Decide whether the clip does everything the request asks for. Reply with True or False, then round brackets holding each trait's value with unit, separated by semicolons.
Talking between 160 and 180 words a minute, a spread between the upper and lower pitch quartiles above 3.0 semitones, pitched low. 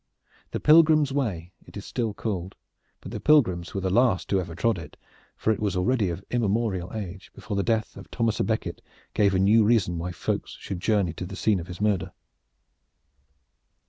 False (195 wpm; 3.9 semitones; 100 Hz)